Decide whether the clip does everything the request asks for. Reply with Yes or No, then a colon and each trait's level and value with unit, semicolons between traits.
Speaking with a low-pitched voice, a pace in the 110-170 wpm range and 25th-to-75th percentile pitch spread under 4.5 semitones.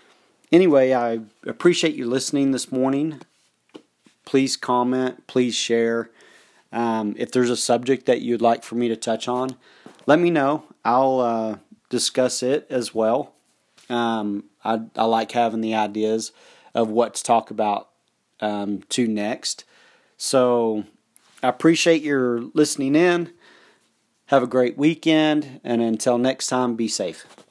Yes: low, 125 Hz; average, 140 wpm; average, 2.8 semitones